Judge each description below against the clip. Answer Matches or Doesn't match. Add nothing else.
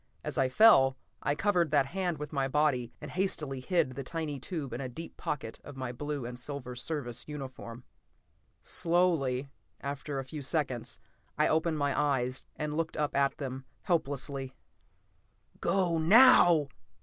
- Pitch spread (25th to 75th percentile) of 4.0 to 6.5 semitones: Doesn't match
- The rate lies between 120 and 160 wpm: Matches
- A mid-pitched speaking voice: Matches